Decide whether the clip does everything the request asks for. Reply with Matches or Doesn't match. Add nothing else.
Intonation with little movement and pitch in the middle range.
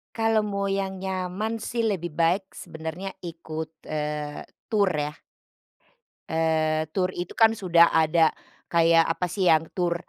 Doesn't match